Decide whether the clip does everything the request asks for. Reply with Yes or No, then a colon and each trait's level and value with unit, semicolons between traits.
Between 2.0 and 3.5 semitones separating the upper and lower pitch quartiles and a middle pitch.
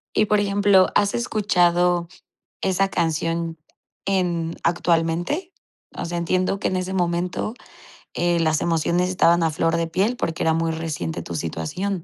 Yes: narrow, 2.5 semitones; medium, 175 Hz